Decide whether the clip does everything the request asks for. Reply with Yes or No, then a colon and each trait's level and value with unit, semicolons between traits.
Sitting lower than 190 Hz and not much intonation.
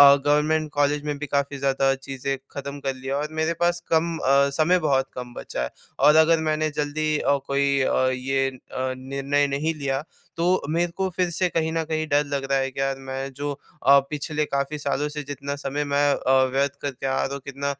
Yes: medium, 140 Hz; narrow, 2.1 semitones